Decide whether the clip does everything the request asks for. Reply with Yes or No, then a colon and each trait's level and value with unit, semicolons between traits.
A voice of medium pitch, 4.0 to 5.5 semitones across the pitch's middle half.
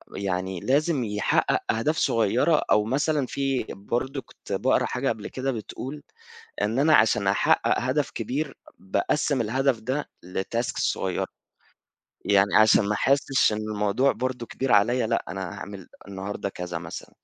No: low, 115 Hz; average, 4.9 semitones